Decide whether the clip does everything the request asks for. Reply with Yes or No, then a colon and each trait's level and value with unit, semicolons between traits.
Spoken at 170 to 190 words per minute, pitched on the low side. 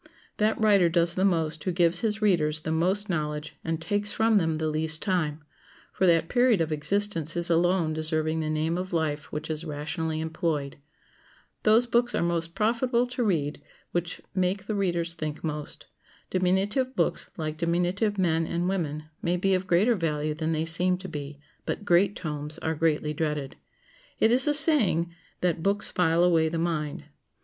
No: average, 175 wpm; medium, 170 Hz